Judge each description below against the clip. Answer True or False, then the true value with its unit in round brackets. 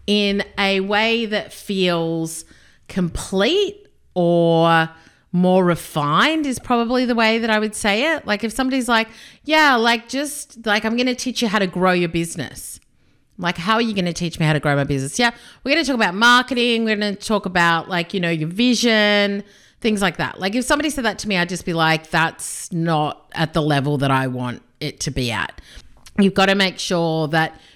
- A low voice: False (195 Hz)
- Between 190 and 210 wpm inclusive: True (200 wpm)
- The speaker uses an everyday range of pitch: False (5.7 semitones)